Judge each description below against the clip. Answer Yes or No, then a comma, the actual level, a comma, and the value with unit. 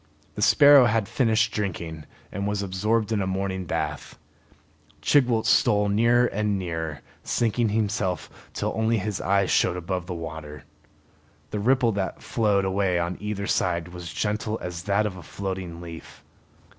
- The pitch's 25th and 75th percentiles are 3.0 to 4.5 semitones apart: Yes, average, 3.4 semitones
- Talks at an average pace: Yes, average, 150 wpm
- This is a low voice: Yes, low, 100 Hz